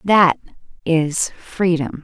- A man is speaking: No, female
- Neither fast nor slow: No, slow, 90 wpm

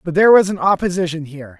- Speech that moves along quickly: Yes, fast, 225 wpm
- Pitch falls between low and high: Yes, medium, 175 Hz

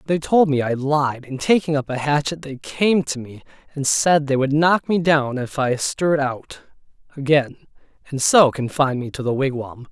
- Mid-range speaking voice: Yes, medium, 145 Hz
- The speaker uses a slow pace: No, average, 200 wpm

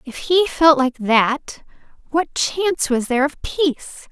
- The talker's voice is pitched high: Yes, very high, 290 Hz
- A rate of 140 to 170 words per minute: Yes, average, 160 wpm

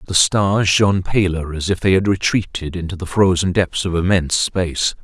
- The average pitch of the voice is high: No, very low, 90 Hz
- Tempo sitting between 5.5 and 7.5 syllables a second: No, 5.2 syllables/s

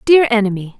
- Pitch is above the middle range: Yes, high, 230 Hz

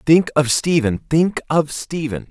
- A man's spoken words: Yes, male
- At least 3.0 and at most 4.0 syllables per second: Yes, 3.8 syllables/s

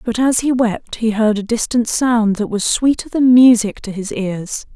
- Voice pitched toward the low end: No, high, 225 Hz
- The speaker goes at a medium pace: No, fast, 215 wpm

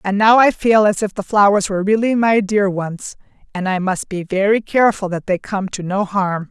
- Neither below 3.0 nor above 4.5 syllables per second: No, 5.1 syllables/s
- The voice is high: Yes, high, 200 Hz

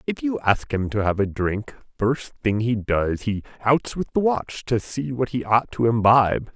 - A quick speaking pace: Yes, fast, 220 wpm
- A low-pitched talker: Yes, low, 115 Hz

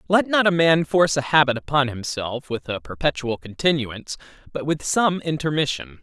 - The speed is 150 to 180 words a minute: Yes, average, 170 wpm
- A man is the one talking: Yes, male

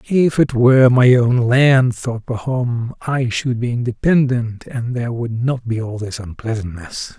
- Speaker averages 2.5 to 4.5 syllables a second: Yes, 4.2 syllables/s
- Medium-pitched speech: No, low, 120 Hz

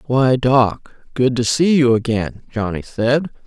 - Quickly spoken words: No, average, 155 wpm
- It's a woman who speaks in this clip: Yes, female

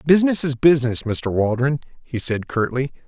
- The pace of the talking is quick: No, average, 155 wpm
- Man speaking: Yes, male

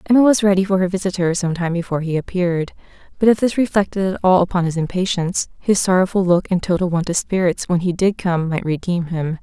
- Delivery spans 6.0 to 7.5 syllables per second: Yes, 6.2 syllables/s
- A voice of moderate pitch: Yes, medium, 180 Hz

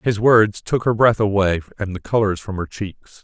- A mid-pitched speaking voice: No, low, 105 Hz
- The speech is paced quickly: Yes, fast, 225 wpm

